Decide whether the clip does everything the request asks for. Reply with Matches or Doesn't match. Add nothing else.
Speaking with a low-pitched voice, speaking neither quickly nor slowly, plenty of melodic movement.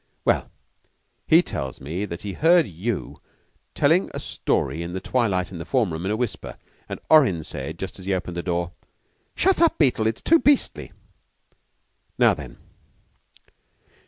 Matches